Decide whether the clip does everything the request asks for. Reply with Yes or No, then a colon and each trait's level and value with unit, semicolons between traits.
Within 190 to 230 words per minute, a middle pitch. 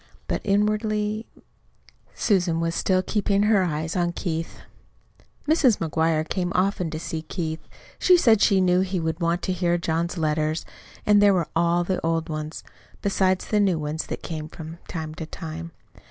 No: average, 170 wpm; medium, 175 Hz